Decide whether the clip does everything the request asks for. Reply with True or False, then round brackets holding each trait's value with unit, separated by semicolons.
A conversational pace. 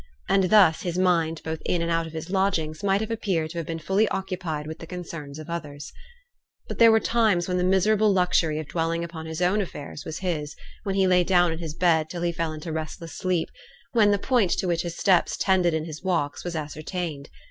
False (225 wpm)